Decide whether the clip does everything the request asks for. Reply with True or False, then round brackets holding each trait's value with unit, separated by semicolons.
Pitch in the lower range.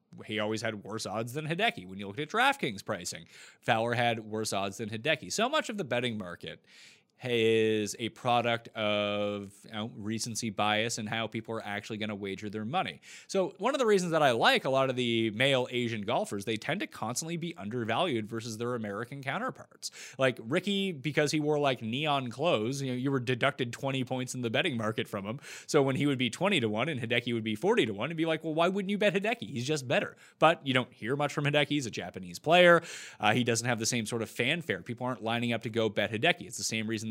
True (120 Hz)